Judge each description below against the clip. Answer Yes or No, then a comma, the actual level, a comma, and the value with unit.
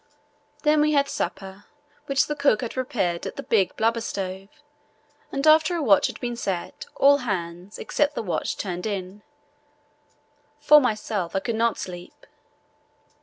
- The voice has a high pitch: Yes, high, 220 Hz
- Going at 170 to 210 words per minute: No, average, 155 wpm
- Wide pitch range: Yes, wide, 6.6 semitones